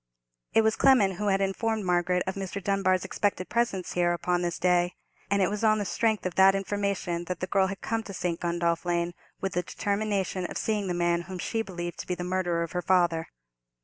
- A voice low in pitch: No, medium, 185 Hz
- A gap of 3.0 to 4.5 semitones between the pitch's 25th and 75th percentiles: No, narrow, 2.4 semitones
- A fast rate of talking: Yes, fast, 220 wpm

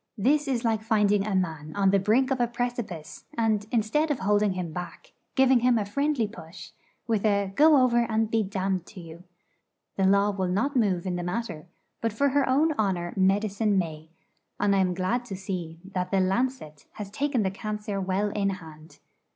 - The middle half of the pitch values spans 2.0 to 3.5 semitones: No, average, 4.0 semitones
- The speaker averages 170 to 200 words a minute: Yes, average, 195 wpm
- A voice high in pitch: Yes, high, 205 Hz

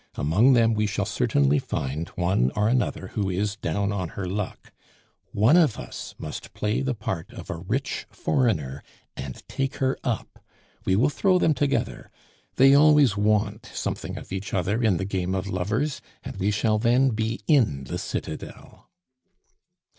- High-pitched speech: No, low, 105 Hz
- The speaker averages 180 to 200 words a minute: No, average, 165 wpm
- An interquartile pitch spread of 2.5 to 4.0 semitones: No, average, 5.1 semitones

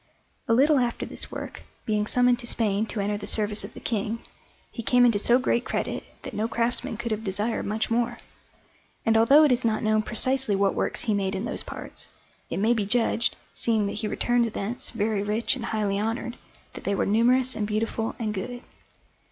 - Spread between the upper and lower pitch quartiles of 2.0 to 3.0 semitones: Yes, narrow, 2.4 semitones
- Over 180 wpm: Yes, fast, 205 wpm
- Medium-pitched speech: No, high, 225 Hz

